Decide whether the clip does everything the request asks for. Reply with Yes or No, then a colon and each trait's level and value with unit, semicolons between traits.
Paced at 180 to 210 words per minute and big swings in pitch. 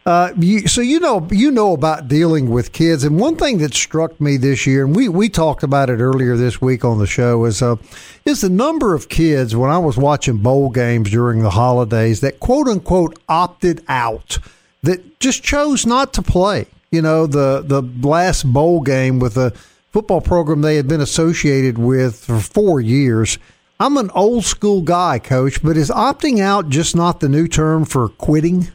Yes: average, 195 wpm; wide, 5.8 semitones